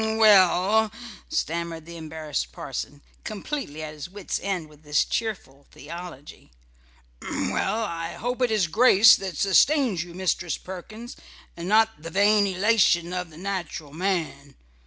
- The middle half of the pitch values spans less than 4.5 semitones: No, average, 4.9 semitones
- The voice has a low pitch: No, medium, 180 Hz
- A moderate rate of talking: Yes, average, 155 wpm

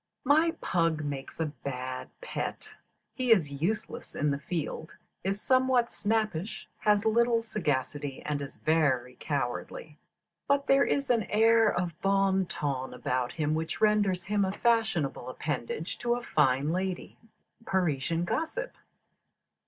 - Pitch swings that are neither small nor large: No, wide, 7.2 semitones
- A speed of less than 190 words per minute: Yes, slow, 135 wpm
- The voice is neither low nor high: Yes, medium, 175 Hz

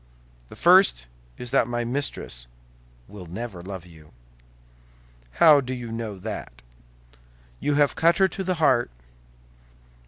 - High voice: No, low, 120 Hz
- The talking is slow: Yes, slow, 130 wpm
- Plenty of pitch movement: Yes, wide, 7.9 semitones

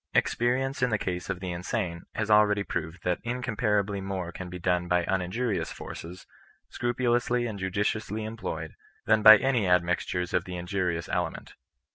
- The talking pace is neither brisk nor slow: Yes, average, 165 wpm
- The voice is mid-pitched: No, low, 100 Hz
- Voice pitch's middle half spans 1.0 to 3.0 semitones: No, average, 3.8 semitones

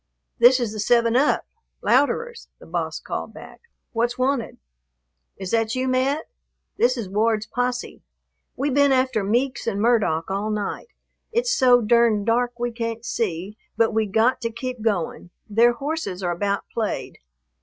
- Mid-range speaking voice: No, high, 235 Hz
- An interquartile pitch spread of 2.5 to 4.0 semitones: Yes, average, 3.1 semitones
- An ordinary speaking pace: Yes, average, 155 wpm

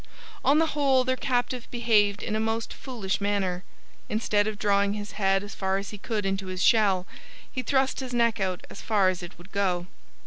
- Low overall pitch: No, high, 205 Hz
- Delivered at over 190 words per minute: Yes, fast, 205 wpm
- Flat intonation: No, average, 3.7 semitones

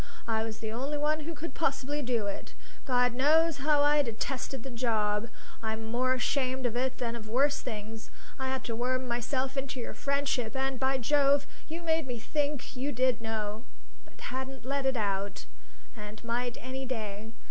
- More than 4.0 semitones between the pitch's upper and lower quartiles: No, average, 3.5 semitones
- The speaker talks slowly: No, average, 180 wpm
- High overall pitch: Yes, very high, 255 Hz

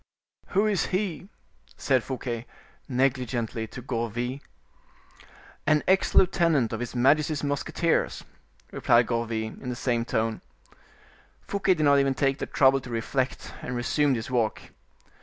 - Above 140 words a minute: No, slow, 135 wpm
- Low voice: Yes, low, 130 Hz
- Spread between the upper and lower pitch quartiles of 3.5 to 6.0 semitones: Yes, average, 4.0 semitones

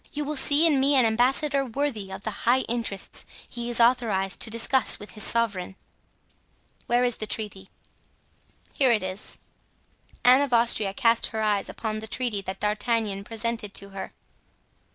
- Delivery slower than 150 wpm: No, average, 165 wpm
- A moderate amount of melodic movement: Yes, average, 3.2 semitones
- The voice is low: No, high, 230 Hz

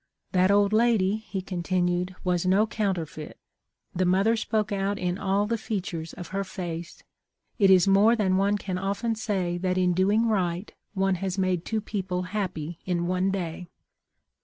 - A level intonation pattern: Yes, narrow, 2.2 semitones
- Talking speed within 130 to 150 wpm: No, average, 175 wpm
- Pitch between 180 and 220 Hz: Yes, high, 190 Hz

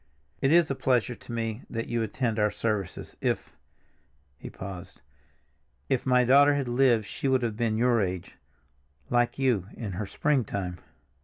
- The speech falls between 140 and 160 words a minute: Yes, average, 155 wpm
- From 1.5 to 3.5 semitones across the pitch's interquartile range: No, average, 4.3 semitones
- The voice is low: Yes, low, 115 Hz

